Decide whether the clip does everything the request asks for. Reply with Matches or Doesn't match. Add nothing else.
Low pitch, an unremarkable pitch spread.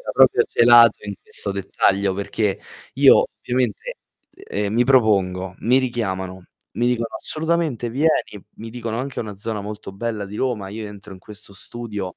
Matches